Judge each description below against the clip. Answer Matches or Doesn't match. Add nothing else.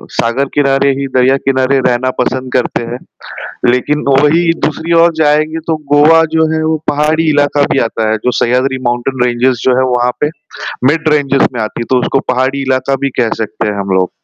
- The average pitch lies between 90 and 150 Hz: Matches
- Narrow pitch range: Doesn't match